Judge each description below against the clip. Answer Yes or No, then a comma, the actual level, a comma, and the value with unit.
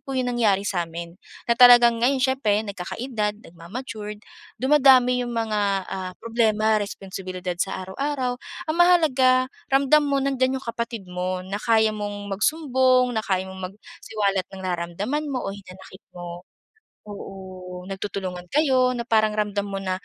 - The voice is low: No, high, 215 Hz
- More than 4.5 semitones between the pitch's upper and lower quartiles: Yes, average, 5.1 semitones